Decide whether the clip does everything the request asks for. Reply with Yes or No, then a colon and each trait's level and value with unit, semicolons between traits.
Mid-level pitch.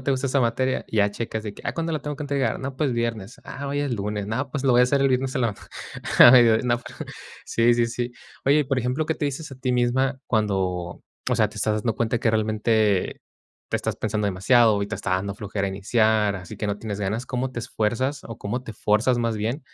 No: low, 120 Hz